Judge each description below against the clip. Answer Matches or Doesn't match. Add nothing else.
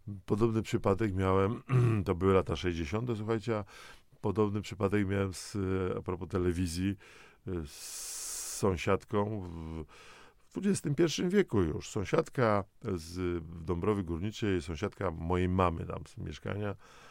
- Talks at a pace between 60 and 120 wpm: Matches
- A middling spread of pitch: Matches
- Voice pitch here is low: Matches